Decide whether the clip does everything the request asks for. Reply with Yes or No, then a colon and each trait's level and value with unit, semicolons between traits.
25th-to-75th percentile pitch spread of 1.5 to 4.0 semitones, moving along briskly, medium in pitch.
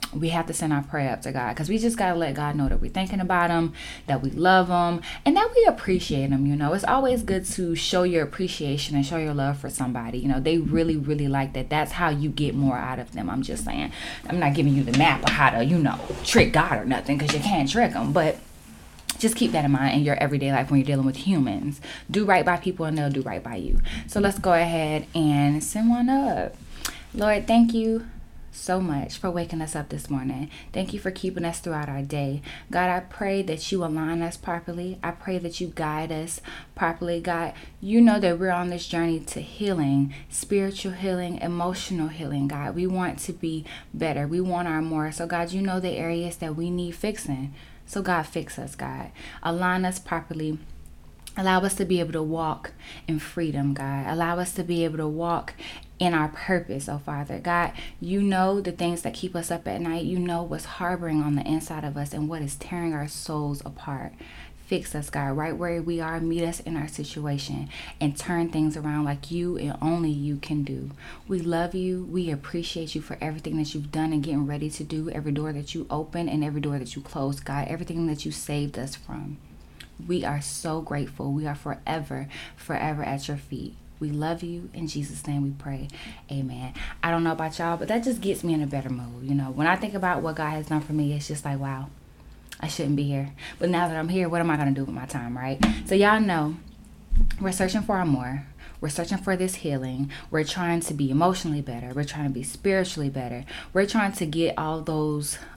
Yes: average, 3.6 semitones; fast, 225 wpm; medium, 160 Hz